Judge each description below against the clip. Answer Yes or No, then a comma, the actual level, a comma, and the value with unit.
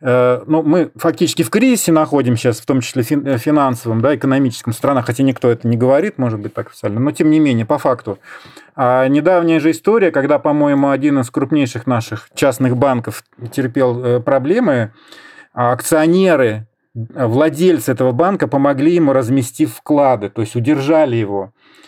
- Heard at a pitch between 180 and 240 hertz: No, low, 135 Hz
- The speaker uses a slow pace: No, average, 155 wpm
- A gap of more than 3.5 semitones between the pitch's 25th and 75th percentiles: Yes, average, 3.9 semitones